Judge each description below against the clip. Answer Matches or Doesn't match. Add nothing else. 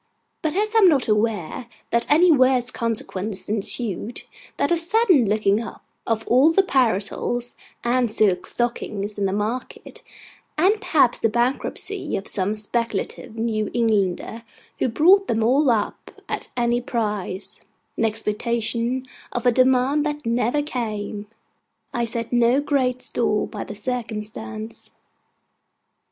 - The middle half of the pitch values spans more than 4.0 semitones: Doesn't match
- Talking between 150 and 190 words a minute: Doesn't match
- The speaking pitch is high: Matches